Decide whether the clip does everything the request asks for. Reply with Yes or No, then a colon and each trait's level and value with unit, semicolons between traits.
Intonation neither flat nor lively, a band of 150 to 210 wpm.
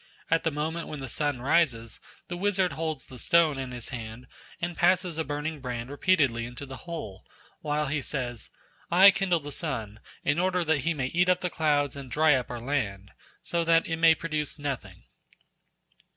Yes: average, 4.6 semitones; average, 190 wpm